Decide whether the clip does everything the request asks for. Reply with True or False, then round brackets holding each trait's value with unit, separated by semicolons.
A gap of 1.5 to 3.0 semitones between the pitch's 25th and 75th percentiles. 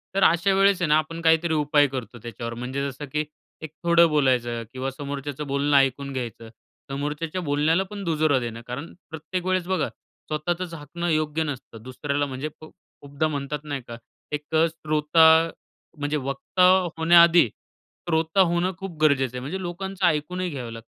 False (3.5 semitones)